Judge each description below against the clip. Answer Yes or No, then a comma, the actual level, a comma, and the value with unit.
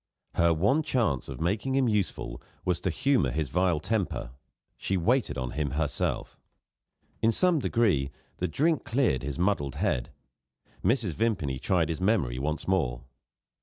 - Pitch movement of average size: No, wide, 7.9 semitones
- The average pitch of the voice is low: Yes, very low, 90 Hz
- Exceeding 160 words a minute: No, average, 150 wpm